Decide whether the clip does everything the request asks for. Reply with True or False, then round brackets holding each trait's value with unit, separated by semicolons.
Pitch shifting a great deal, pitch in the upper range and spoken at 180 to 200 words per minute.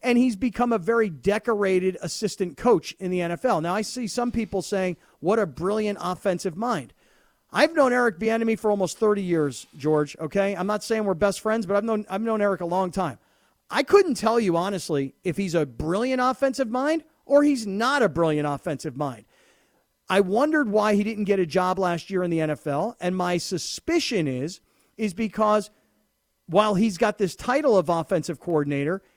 False (4.3 semitones; 200 Hz; 190 wpm)